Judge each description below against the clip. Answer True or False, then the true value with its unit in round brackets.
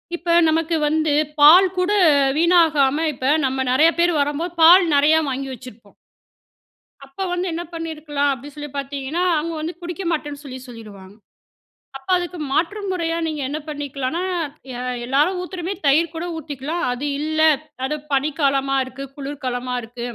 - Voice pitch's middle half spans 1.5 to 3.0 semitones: False (3.6 semitones)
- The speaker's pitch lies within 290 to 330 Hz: True (295 Hz)